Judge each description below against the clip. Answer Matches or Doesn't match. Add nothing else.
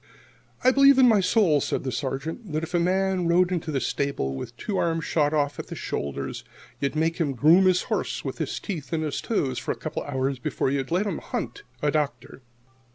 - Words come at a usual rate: Doesn't match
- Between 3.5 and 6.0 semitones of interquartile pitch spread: Matches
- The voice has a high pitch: Doesn't match